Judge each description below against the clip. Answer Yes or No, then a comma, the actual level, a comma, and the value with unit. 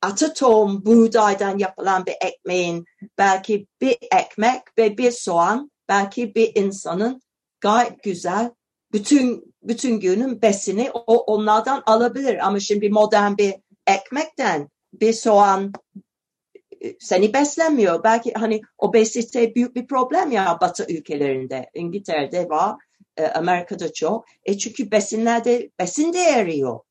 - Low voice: No, high, 215 Hz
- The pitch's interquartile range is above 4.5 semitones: No, average, 3.7 semitones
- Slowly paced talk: No, average, 110 wpm